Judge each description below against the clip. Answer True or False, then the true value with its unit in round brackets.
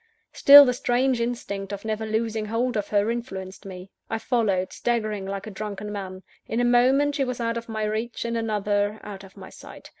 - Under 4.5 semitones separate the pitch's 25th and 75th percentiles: True (2.9 semitones)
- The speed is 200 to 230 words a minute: True (205 wpm)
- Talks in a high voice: True (220 Hz)